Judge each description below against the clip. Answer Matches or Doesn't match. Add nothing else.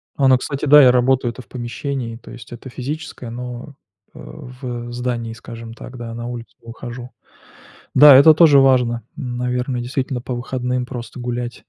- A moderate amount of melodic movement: Doesn't match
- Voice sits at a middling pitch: Doesn't match